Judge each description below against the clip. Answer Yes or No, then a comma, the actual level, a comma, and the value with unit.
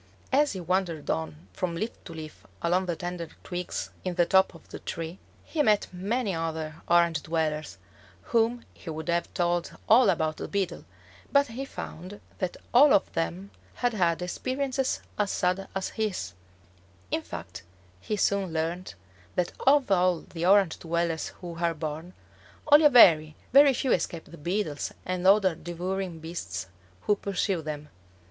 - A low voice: No, medium, 175 Hz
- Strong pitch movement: No, average, 3.7 semitones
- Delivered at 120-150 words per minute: No, average, 160 wpm